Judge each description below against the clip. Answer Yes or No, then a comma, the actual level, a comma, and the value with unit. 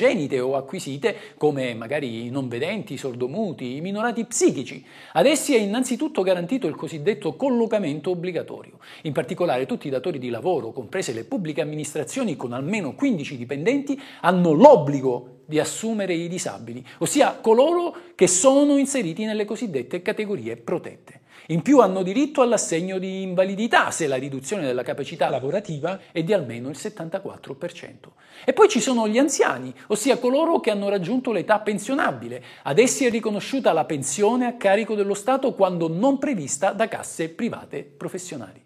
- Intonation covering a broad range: Yes, wide, 7.8 semitones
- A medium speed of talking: Yes, average, 155 wpm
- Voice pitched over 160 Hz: Yes, high, 190 Hz